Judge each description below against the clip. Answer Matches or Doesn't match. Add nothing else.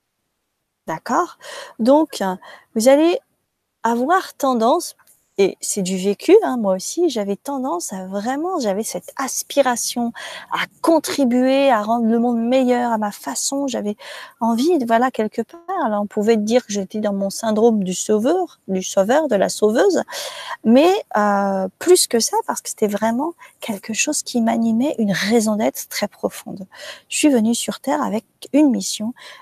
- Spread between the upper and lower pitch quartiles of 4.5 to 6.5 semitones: Matches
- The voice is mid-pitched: Doesn't match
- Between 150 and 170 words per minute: Matches